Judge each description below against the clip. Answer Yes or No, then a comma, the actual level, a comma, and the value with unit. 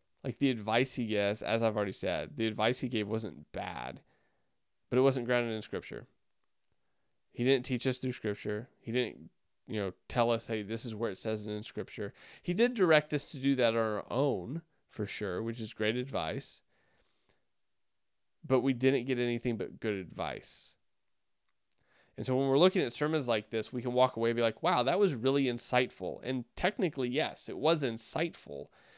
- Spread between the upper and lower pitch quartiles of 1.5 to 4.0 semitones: Yes, average, 3.4 semitones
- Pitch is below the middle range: Yes, low, 120 Hz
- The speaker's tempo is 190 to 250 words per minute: Yes, average, 195 wpm